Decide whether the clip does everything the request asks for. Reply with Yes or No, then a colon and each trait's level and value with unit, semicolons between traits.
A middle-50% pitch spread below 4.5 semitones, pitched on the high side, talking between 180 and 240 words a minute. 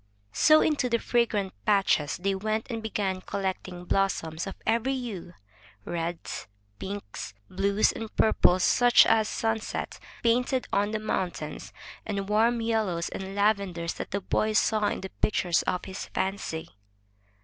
No: average, 3.2 semitones; high, 200 Hz; average, 145 wpm